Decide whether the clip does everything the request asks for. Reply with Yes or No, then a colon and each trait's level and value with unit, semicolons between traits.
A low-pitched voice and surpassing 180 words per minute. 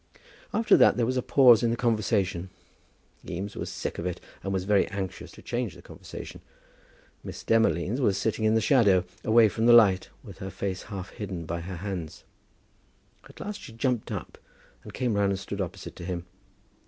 Yes: low, 100 Hz; average, 190 wpm